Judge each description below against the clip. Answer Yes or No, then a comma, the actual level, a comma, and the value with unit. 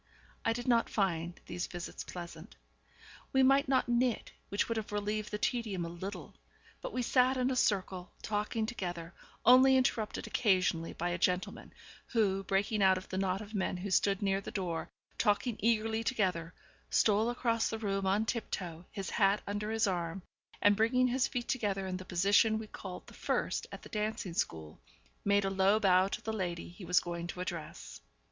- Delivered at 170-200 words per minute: Yes, average, 185 wpm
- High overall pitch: Yes, high, 200 Hz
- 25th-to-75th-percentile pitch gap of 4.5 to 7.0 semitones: No, average, 3.4 semitones